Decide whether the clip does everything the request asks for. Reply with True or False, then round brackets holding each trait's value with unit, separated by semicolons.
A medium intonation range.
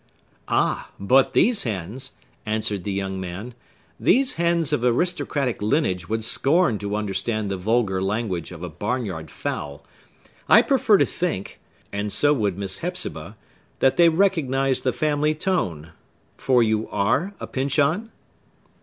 False (7.3 semitones)